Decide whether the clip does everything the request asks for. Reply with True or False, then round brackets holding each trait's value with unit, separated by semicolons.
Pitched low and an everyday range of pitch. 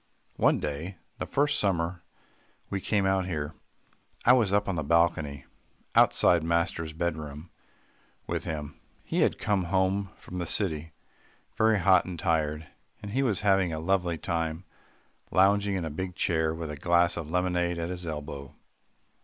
True (85 Hz; 3.2 semitones)